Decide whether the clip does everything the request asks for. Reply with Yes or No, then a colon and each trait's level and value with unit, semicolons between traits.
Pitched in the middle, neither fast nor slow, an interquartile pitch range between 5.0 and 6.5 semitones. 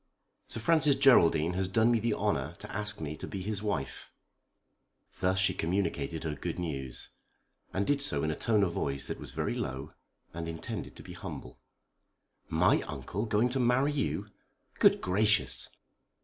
No: very low, 95 Hz; average, 170 wpm; wide, 5.6 semitones